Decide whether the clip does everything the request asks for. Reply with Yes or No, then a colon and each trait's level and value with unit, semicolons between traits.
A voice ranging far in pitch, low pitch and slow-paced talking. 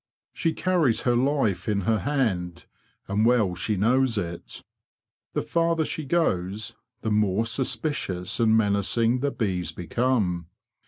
Yes: wide, 5.7 semitones; low, 110 Hz; slow, 130 wpm